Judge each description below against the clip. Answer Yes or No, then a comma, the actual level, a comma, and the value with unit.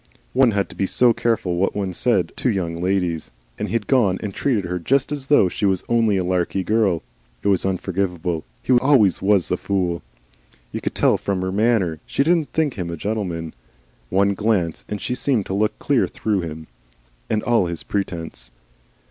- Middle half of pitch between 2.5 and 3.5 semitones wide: No, average, 4.2 semitones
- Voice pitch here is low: Yes, low, 100 Hz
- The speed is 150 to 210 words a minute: Yes, average, 190 wpm